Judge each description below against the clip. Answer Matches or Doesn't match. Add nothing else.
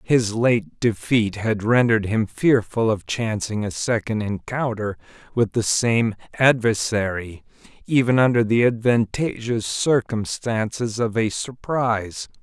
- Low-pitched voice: Matches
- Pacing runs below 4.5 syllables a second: Matches